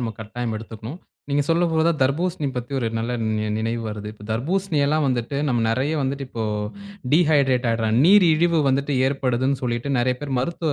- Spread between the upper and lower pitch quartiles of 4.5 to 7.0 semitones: Yes, average, 4.8 semitones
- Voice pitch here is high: No, low, 135 Hz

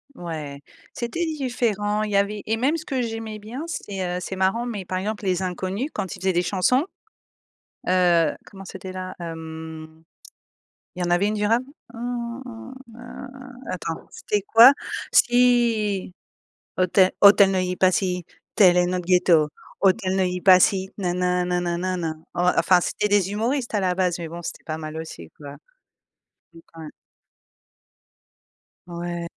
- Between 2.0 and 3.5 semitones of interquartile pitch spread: No, average, 4.0 semitones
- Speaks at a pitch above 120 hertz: Yes, high, 190 Hz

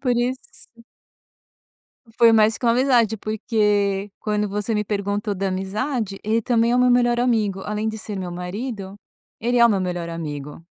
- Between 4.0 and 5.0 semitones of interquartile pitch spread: No, average, 3.3 semitones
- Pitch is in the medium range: No, high, 210 Hz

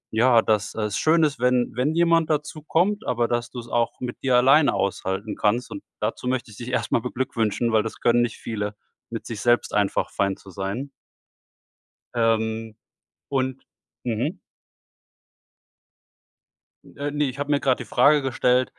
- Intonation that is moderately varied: Yes, average, 3.8 semitones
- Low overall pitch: Yes, low, 120 Hz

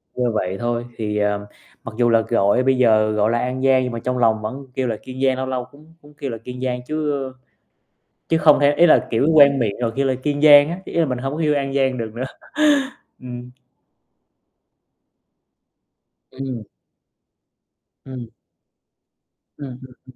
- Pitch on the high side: No, low, 130 Hz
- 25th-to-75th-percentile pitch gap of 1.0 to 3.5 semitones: Yes, average, 2.9 semitones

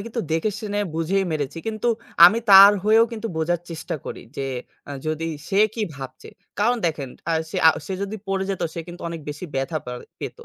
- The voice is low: No, medium, 175 Hz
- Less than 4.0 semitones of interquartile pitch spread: No, average, 4.7 semitones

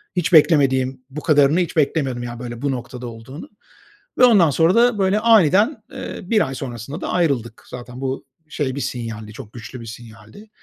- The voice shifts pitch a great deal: Yes, wide, 6.0 semitones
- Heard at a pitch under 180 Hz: Yes, low, 135 Hz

